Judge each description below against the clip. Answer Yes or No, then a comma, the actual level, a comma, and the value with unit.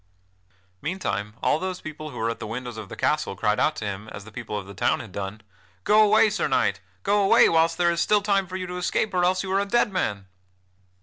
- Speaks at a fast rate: Yes, fast, 250 wpm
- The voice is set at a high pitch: No, medium, 160 Hz